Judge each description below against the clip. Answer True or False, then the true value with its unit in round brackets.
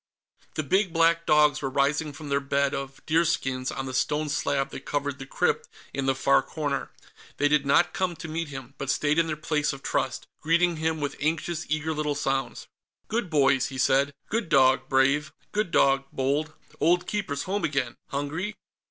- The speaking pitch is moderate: True (145 Hz)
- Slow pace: False (185 wpm)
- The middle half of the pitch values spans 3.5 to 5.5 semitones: False (2.8 semitones)